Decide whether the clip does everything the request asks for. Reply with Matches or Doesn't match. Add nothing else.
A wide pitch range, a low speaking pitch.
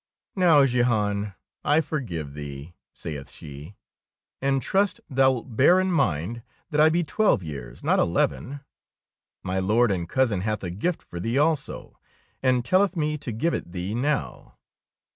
Matches